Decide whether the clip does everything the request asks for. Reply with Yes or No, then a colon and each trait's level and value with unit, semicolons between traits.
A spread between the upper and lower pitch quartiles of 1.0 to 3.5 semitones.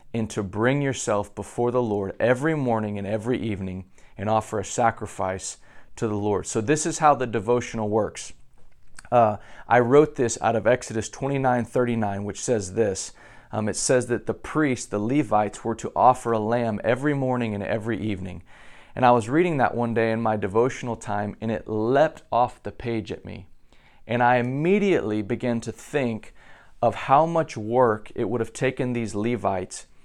Yes: average, 3.1 semitones